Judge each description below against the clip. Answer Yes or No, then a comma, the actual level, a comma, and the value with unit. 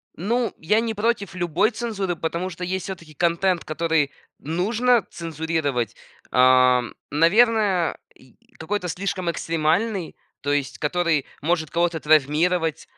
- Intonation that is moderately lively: Yes, average, 3.9 semitones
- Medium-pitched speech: Yes, medium, 170 Hz